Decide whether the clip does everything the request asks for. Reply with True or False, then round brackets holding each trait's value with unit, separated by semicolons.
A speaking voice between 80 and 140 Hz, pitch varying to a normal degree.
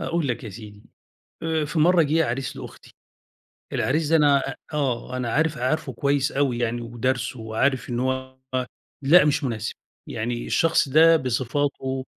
True (135 Hz; 4.0 semitones)